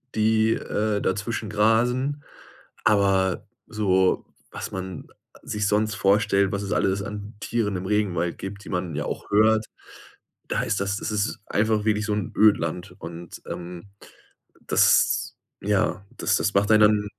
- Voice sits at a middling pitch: No, low, 105 Hz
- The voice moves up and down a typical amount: No, narrow, 2.0 semitones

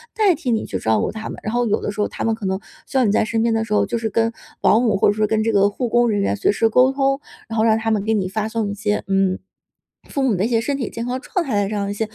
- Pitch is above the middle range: Yes, high, 220 Hz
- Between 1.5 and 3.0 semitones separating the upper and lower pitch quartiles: Yes, narrow, 2.4 semitones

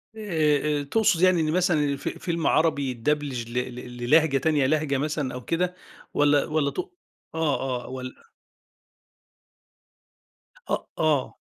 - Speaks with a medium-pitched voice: Yes, medium, 150 Hz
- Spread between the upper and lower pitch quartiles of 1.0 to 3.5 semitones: Yes, average, 3.1 semitones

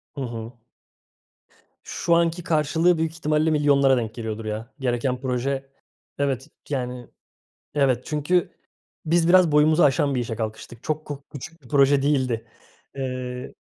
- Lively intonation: No, average, 3.7 semitones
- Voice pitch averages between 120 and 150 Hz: Yes, medium, 140 Hz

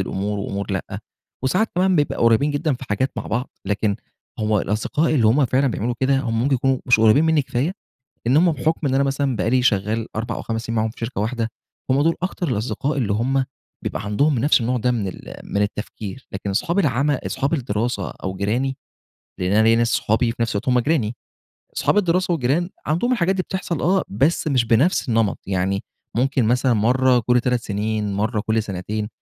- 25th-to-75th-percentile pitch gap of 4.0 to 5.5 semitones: Yes, average, 4.6 semitones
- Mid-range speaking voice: No, low, 125 Hz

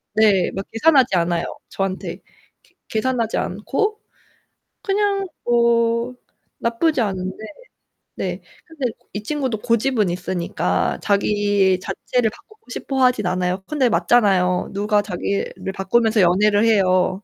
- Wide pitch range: No, average, 4.6 semitones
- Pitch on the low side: No, high, 215 Hz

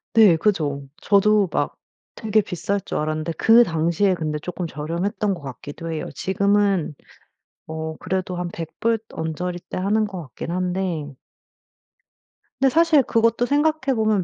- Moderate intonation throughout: Yes, average, 4.8 semitones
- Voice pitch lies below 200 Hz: Yes, medium, 185 Hz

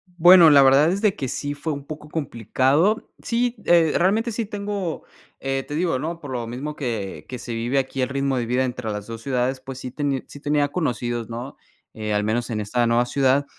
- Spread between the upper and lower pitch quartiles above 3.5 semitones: Yes, average, 4.6 semitones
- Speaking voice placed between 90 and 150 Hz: Yes, low, 135 Hz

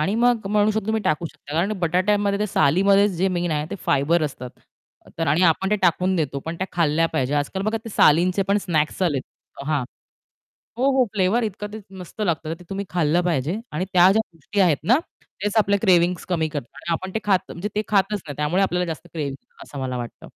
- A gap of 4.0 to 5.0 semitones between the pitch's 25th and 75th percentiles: Yes, average, 4.5 semitones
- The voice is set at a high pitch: No, medium, 180 Hz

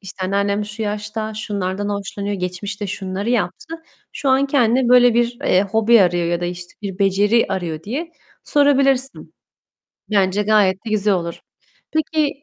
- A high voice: Yes, high, 205 Hz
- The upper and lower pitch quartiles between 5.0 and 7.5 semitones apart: No, average, 3.9 semitones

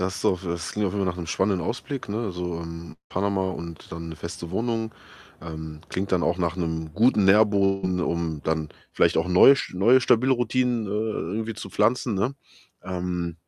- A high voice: No, very low, 95 Hz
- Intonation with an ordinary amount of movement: Yes, average, 4.2 semitones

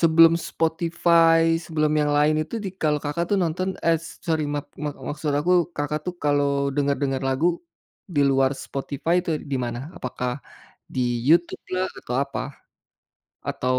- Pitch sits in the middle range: Yes, medium, 150 Hz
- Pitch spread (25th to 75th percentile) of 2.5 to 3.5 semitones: Yes, average, 2.8 semitones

